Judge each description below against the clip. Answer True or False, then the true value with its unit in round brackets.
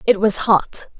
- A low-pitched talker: False (205 Hz)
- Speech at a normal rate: True (180 wpm)